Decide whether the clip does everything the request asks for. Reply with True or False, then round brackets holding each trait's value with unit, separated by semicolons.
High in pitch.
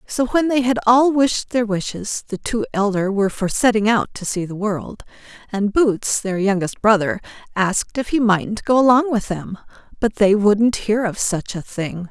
True (215 Hz)